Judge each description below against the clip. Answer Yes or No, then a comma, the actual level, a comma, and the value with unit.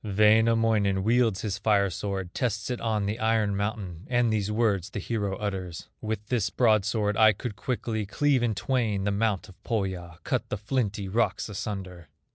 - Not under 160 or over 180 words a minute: Yes, average, 170 wpm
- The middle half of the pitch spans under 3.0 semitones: Yes, narrow, 2.4 semitones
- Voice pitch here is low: Yes, low, 105 Hz